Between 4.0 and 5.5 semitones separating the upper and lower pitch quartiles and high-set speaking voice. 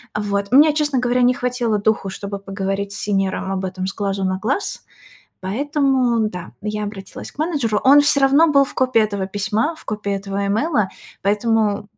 Yes: average, 4.7 semitones; high, 215 Hz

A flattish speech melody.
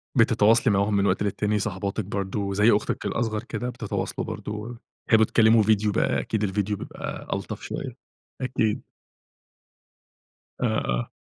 Yes: narrow, 1.9 semitones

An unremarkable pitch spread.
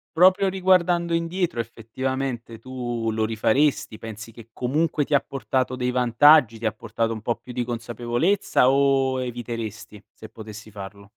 Yes: average, 3.8 semitones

